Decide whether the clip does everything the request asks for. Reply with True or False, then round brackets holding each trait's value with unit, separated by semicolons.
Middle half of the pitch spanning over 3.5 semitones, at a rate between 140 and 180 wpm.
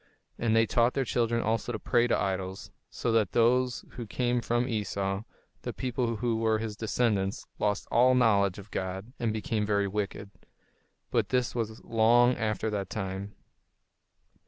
False (2.8 semitones; 160 wpm)